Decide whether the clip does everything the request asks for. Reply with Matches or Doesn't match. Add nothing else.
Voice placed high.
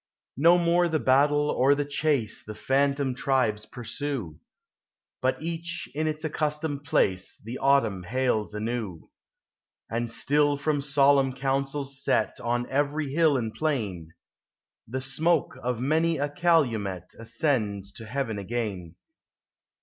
Doesn't match